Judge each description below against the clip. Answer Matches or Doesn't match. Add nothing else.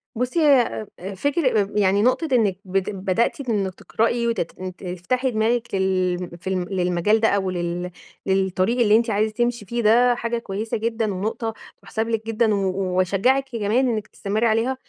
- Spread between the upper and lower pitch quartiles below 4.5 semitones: Matches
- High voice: Matches